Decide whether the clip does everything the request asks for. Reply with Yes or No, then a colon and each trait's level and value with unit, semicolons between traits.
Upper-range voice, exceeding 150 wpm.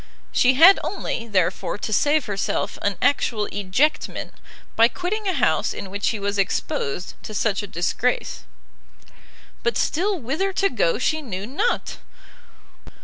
No: high, 240 Hz; average, 145 wpm